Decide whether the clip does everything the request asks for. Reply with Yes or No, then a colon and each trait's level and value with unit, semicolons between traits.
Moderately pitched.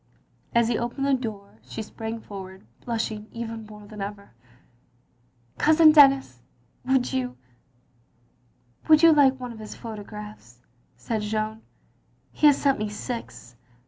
No: high, 220 Hz